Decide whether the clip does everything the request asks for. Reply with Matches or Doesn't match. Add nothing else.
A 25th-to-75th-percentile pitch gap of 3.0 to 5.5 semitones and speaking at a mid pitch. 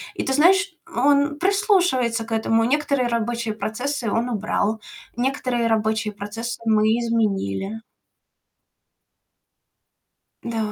Doesn't match